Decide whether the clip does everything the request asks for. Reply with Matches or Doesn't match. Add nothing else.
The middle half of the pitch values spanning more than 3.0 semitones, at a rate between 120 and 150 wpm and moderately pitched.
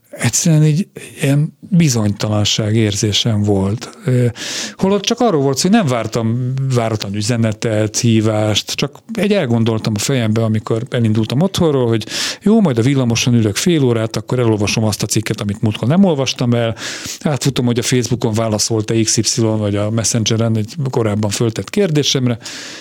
Doesn't match